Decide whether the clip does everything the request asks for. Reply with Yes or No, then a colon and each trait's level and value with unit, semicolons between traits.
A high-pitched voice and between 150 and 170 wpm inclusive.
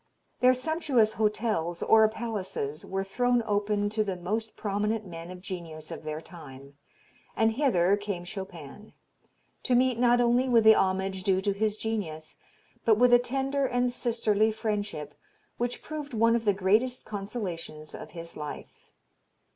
Yes: high, 210 Hz; average, 155 wpm